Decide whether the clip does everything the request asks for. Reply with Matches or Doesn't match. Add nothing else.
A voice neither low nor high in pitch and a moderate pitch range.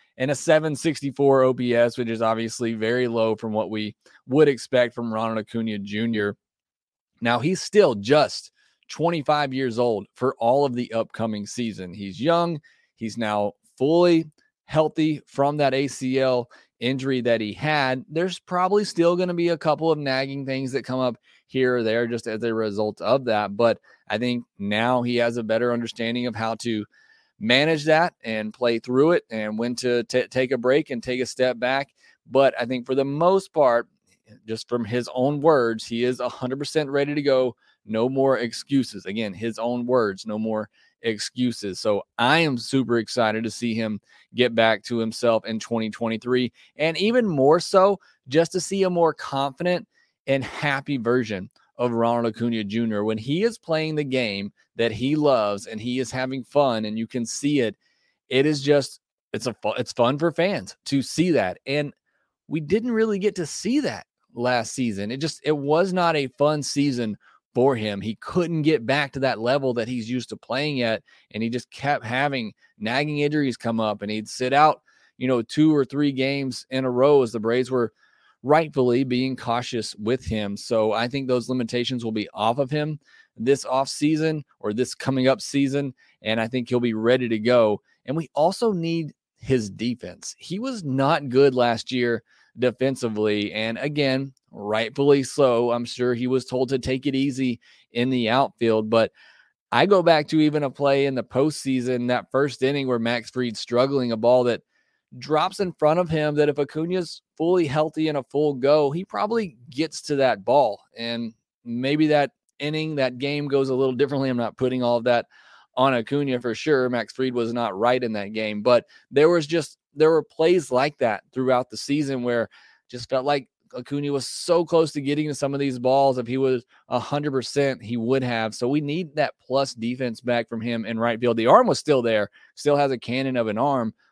Doesn't match